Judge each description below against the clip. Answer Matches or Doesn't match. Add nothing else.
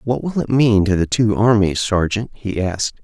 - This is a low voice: Matches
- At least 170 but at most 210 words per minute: Doesn't match